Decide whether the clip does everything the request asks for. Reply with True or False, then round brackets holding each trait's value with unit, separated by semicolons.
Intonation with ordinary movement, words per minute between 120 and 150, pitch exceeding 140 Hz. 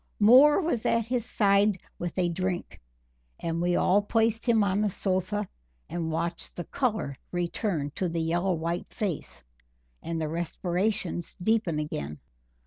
True (4.0 semitones; 145 wpm; 185 Hz)